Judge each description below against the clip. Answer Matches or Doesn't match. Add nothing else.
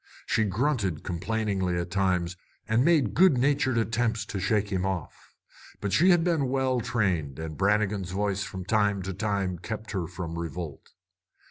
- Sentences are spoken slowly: Doesn't match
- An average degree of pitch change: Matches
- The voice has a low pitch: Matches